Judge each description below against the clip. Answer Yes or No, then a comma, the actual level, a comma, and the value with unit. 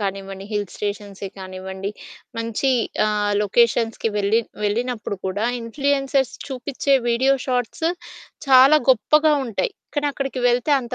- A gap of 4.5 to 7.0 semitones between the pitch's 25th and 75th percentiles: Yes, average, 4.8 semitones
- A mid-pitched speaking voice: No, high, 230 Hz